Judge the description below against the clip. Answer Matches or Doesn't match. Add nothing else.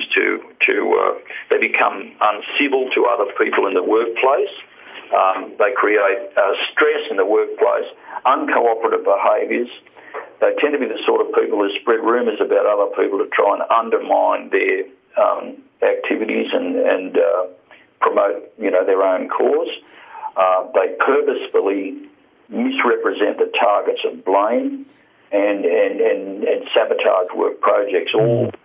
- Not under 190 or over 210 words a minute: Doesn't match